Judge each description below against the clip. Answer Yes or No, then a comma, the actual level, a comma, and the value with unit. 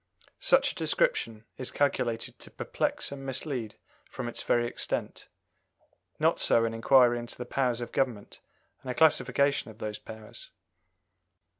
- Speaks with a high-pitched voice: No, low, 120 Hz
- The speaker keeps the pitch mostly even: No, average, 3.0 semitones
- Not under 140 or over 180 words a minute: Yes, average, 145 wpm